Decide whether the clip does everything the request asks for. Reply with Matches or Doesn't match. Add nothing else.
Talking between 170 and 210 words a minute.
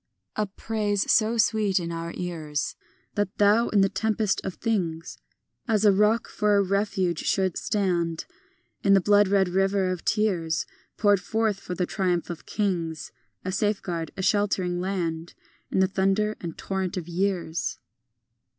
Doesn't match